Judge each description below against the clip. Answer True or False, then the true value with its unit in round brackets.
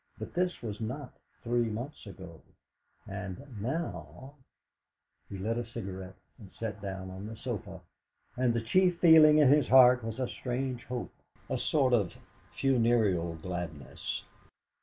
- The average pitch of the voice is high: False (115 Hz)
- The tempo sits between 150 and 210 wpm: False (140 wpm)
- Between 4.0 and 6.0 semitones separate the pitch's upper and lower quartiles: True (5.2 semitones)